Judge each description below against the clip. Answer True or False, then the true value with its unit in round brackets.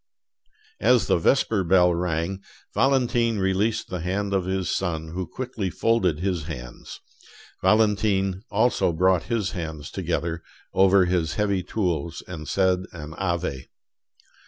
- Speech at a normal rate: False (130 wpm)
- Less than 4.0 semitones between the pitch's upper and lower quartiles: True (3.3 semitones)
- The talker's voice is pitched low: True (95 Hz)